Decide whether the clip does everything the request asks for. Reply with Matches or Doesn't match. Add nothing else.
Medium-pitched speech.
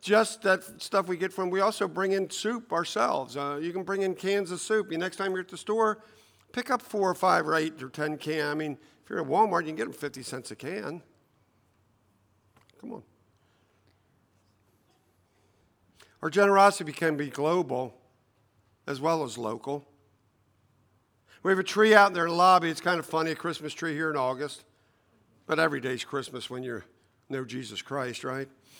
Matches